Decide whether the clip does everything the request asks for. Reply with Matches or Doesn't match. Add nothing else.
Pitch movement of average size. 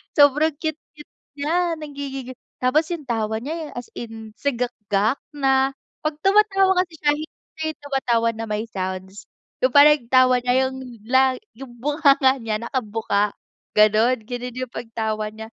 Matches